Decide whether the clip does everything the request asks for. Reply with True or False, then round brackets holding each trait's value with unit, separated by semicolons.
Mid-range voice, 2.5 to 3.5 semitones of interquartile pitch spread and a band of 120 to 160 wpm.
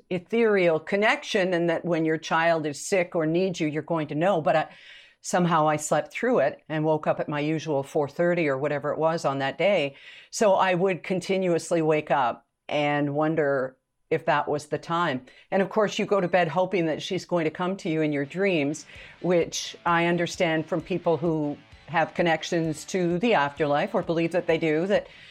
False (165 Hz; 3.0 semitones; 200 wpm)